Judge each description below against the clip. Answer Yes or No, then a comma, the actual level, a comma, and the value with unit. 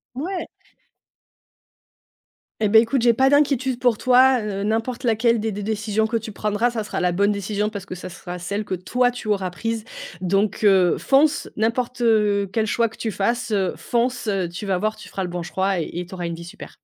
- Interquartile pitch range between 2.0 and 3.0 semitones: No, average, 3.5 semitones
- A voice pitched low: No, high, 215 Hz